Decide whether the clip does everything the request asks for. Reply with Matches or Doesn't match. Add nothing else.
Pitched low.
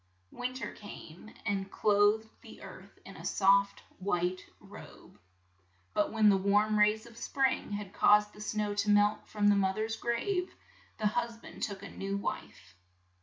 Doesn't match